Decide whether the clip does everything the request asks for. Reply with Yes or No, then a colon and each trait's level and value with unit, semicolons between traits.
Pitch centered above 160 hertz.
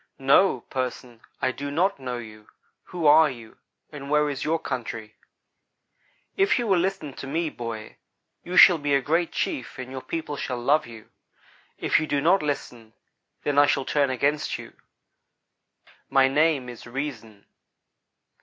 No: medium, 140 Hz